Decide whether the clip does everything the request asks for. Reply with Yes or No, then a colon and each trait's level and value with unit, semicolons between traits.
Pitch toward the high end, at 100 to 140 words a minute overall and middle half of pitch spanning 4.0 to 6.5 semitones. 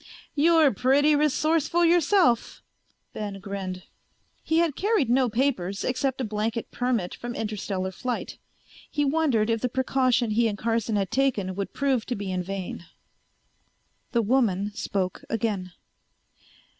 Yes: high, 235 Hz; slow, 135 wpm; wide, 5.4 semitones